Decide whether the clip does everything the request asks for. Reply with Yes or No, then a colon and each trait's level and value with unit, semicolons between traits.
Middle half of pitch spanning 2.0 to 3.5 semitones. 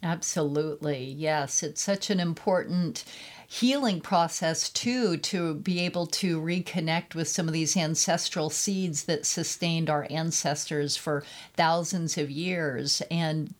Yes: narrow, 2.6 semitones